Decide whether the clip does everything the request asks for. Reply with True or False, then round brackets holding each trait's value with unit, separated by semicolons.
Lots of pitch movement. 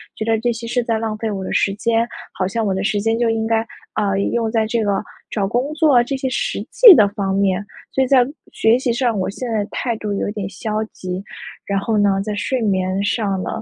False (2.9 semitones)